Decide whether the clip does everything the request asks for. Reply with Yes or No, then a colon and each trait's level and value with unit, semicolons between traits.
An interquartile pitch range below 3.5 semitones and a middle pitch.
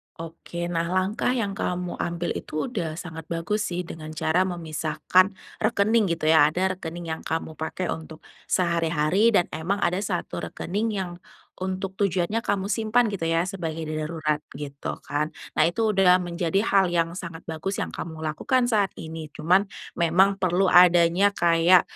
Yes: average, 3.1 semitones; medium, 175 Hz